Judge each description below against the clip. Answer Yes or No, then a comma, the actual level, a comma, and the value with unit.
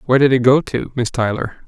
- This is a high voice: No, low, 125 Hz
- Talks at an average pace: No, fast, 250 wpm